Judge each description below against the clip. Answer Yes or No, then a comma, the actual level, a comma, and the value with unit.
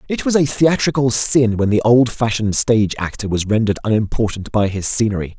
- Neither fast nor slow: Yes, average, 180 wpm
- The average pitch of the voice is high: No, low, 115 Hz